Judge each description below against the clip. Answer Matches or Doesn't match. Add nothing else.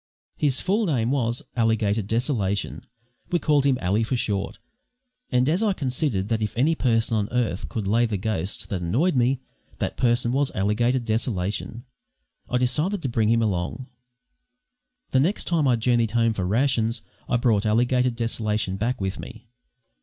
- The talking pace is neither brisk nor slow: Matches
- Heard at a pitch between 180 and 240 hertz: Doesn't match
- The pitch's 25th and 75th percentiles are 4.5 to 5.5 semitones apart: Doesn't match